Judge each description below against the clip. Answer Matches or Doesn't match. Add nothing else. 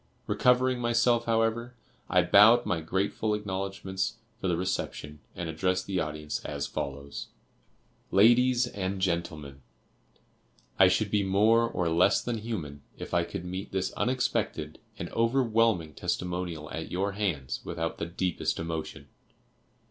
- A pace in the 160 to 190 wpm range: Doesn't match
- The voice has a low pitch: Matches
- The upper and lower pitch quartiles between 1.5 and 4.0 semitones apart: Doesn't match